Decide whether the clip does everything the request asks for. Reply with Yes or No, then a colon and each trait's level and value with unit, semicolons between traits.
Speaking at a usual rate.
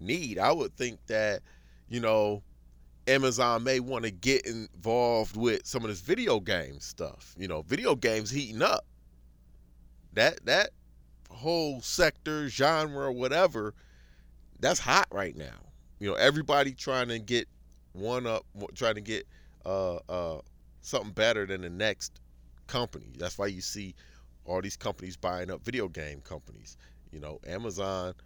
Yes: average, 150 wpm